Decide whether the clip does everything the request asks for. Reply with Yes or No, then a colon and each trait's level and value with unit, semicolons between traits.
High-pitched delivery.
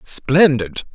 No: medium, 140 Hz